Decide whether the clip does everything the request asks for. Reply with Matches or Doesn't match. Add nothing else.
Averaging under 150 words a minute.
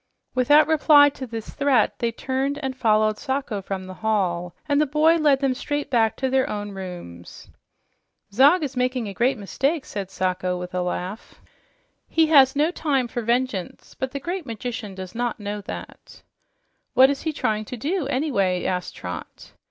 Doesn't match